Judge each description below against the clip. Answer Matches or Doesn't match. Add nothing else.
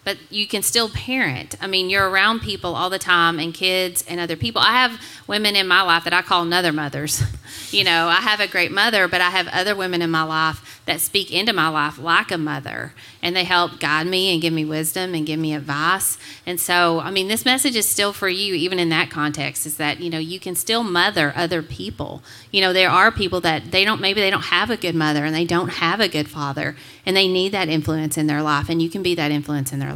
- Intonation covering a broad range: Doesn't match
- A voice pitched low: Doesn't match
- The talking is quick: Matches